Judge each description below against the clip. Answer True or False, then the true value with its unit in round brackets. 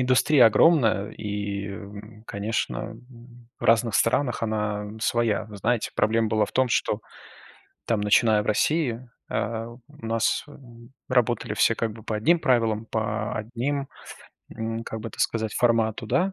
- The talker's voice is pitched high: False (115 Hz)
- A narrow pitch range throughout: True (2.1 semitones)